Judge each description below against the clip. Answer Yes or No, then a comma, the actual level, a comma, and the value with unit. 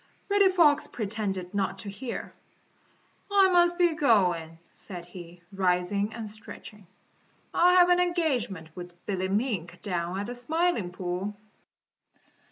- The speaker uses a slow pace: Yes, slow, 130 wpm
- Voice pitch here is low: No, high, 205 Hz